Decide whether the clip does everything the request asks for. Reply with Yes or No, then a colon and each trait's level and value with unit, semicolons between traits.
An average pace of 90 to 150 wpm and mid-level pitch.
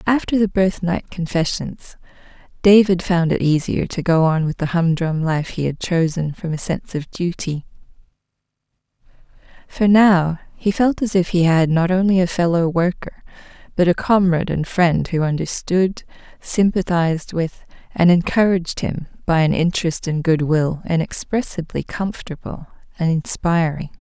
Yes: average, 145 wpm; medium, 175 Hz